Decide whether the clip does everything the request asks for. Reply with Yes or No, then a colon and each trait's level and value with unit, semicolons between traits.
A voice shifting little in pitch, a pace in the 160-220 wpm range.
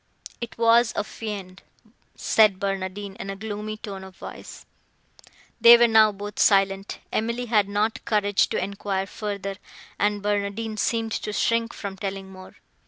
No: narrow, 2.1 semitones; average, 145 wpm